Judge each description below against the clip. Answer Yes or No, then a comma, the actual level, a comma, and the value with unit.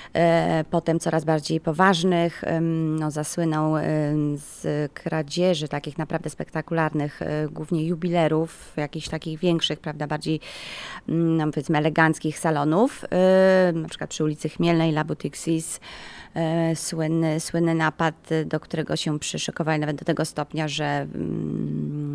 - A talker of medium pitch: Yes, medium, 160 Hz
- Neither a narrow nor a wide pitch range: No, narrow, 1.4 semitones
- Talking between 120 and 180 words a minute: No, slow, 110 wpm